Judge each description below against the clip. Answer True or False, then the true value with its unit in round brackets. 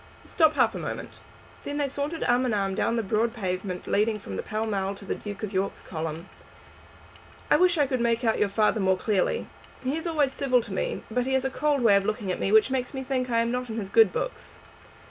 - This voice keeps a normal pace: False (240 wpm)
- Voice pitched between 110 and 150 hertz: False (230 Hz)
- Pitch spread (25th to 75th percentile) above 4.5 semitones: True (4.9 semitones)